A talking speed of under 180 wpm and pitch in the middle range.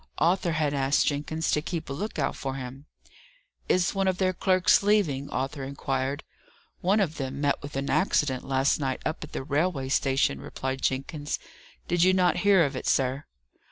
No: average, 185 wpm; medium, 145 Hz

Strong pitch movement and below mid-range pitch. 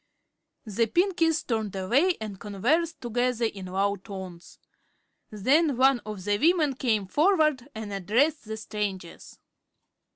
No: wide, 6.6 semitones; high, 225 Hz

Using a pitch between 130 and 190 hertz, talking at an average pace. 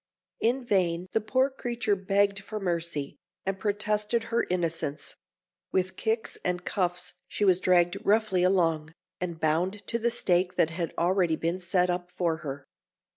Yes: medium, 185 Hz; average, 155 wpm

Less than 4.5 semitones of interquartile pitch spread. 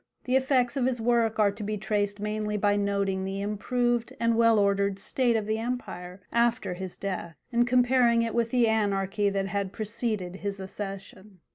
Yes: average, 2.9 semitones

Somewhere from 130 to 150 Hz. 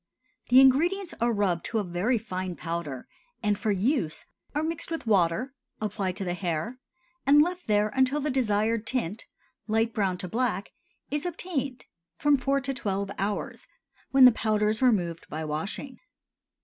No: high, 220 Hz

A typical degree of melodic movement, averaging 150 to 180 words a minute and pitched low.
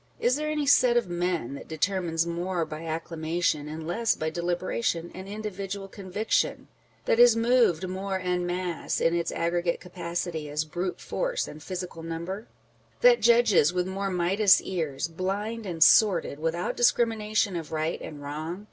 No: average, 3.6 semitones; average, 165 wpm; medium, 180 Hz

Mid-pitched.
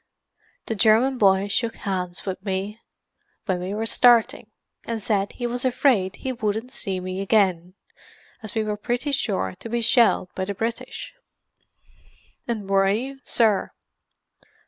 No: high, 215 Hz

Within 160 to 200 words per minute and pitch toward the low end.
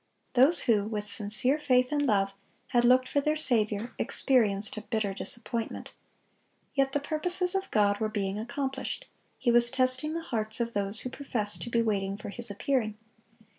No: average, 170 wpm; high, 235 Hz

